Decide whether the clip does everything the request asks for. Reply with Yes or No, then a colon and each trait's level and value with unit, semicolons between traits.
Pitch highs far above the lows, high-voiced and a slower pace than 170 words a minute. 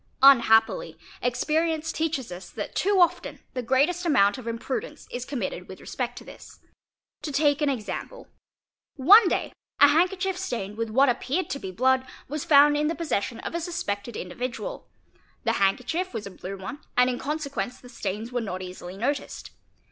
No: wide, 6.1 semitones; very high, 260 Hz; average, 175 wpm